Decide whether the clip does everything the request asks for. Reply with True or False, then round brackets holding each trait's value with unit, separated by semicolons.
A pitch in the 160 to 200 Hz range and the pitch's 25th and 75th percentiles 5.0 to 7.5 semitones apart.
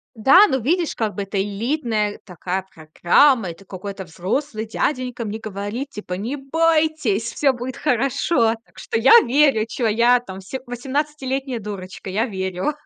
False (230 Hz; 5.3 semitones)